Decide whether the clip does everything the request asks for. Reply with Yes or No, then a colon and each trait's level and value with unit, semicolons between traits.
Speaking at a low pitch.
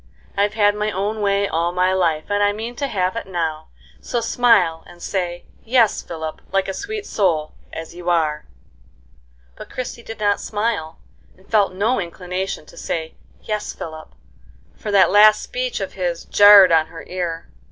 No: high, 195 Hz